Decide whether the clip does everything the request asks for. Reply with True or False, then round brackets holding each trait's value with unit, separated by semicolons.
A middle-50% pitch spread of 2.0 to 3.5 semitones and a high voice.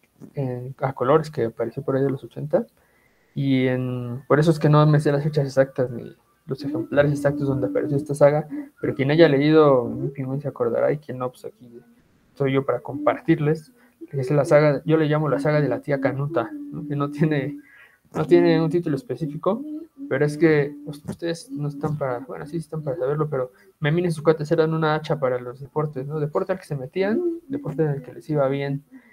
False (2.8 semitones; 145 Hz)